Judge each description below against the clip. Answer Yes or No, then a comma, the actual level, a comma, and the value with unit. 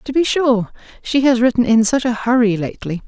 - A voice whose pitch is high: Yes, high, 240 Hz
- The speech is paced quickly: Yes, fast, 215 wpm